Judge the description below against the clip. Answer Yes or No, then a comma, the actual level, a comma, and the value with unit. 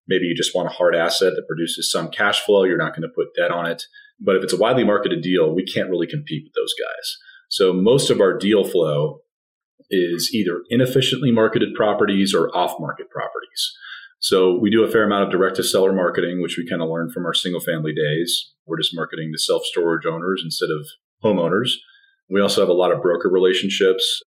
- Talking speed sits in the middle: No, fast, 215 wpm